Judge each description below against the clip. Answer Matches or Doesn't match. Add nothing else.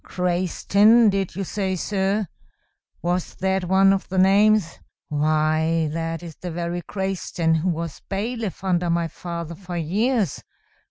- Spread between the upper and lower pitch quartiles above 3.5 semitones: Doesn't match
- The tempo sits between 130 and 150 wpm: Matches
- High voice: Doesn't match